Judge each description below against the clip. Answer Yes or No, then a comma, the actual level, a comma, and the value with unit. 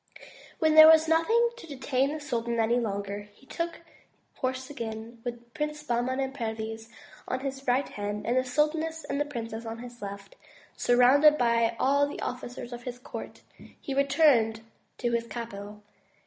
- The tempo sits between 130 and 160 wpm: No, average, 175 wpm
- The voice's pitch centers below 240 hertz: No, high, 245 Hz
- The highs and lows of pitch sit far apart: No, average, 3.9 semitones